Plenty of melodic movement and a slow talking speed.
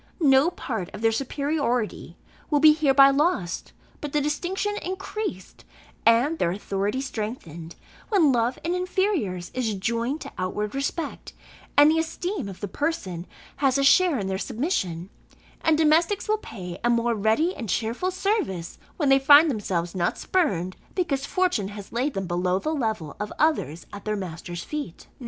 No: wide, 8.2 semitones; average, 160 wpm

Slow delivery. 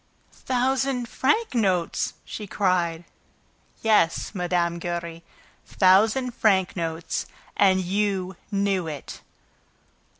Yes: slow, 90 wpm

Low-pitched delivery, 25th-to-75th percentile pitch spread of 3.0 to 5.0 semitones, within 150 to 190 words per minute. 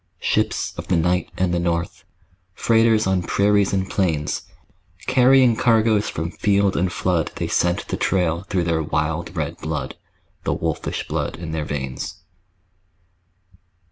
No: very low, 90 Hz; average, 3.7 semitones; average, 140 wpm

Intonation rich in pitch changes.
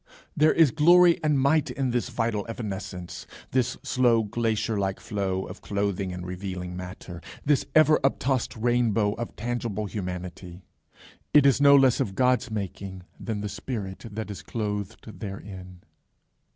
No: average, 4.9 semitones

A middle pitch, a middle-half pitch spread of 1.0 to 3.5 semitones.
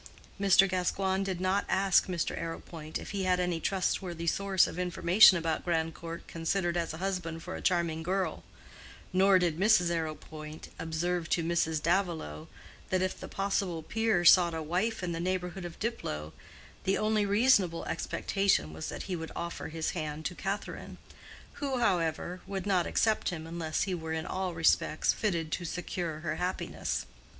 Yes: medium, 175 Hz; average, 2.8 semitones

